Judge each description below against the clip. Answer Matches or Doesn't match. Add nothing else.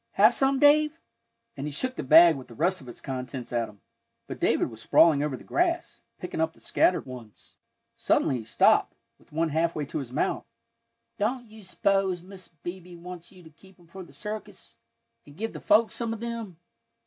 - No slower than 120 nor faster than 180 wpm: Doesn't match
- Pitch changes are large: Matches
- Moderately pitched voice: Matches